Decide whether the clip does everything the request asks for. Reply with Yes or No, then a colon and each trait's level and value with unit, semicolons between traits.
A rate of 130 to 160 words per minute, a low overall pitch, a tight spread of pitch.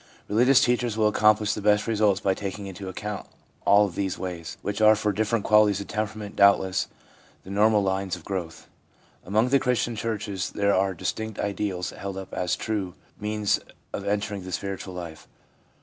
No: average, 180 wpm; low, 100 Hz; narrow, 2.1 semitones